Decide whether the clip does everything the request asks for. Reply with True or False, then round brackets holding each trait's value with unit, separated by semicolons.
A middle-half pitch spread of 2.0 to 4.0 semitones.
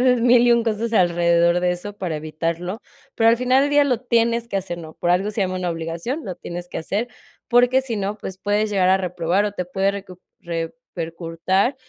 False (5.0 semitones)